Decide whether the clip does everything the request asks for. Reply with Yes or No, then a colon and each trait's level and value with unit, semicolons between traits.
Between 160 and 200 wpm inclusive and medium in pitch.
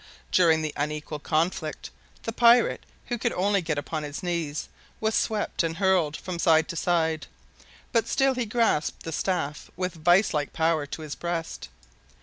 Yes: average, 165 wpm; medium, 165 Hz